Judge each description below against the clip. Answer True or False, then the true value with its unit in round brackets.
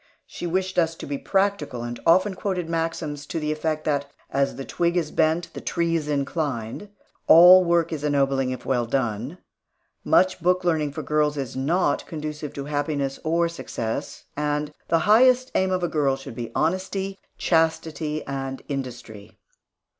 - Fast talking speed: False (160 wpm)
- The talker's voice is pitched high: False (155 Hz)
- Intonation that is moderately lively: True (3.8 semitones)